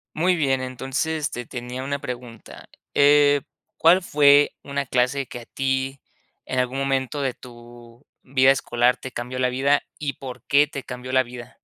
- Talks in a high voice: No, low, 130 Hz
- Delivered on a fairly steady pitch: Yes, narrow, 2.2 semitones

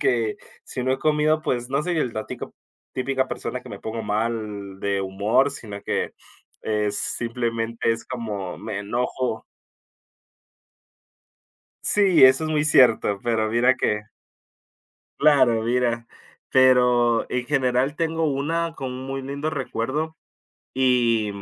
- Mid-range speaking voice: No, low, 125 Hz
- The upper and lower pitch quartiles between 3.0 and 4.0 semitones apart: Yes, average, 3.4 semitones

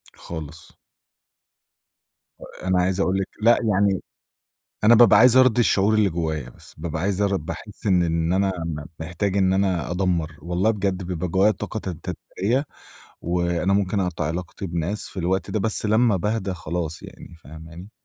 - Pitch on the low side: Yes, very low, 95 Hz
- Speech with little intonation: No, average, 3.2 semitones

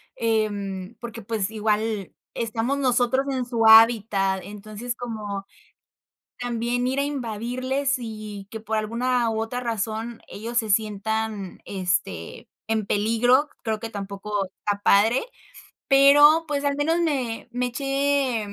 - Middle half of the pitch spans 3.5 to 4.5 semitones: No, average, 3.1 semitones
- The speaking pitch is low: No, high, 225 Hz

